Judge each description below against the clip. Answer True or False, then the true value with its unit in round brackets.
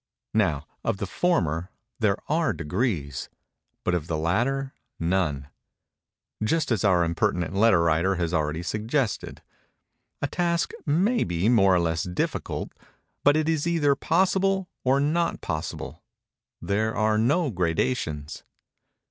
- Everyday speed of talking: False (120 wpm)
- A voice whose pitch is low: True (105 Hz)